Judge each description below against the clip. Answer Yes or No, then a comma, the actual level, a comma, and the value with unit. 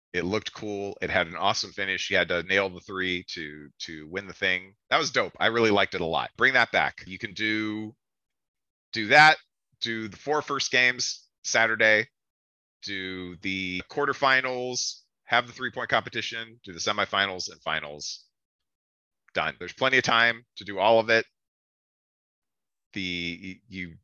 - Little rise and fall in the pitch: No, average, 4.3 semitones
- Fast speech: No, average, 165 wpm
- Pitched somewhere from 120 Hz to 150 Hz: No, low, 100 Hz